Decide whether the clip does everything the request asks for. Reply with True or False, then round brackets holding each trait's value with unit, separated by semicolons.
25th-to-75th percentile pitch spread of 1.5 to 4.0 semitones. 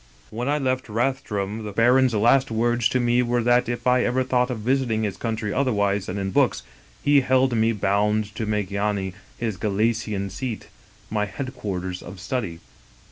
True (3.5 semitones)